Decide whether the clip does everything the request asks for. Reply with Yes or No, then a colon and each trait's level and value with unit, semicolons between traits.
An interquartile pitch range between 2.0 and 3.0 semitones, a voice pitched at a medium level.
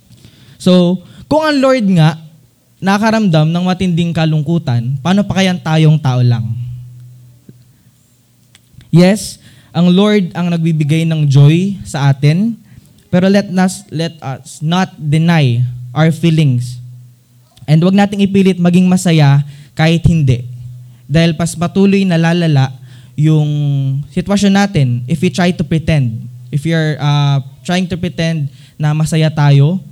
No: average, 5.0 semitones; medium, 155 Hz